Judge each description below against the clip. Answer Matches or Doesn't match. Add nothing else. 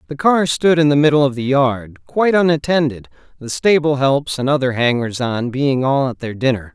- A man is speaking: Matches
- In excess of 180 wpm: Matches